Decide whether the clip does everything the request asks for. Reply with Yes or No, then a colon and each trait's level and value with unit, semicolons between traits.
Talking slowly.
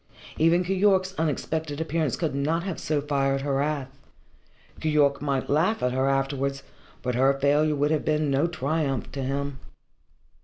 No: average, 160 wpm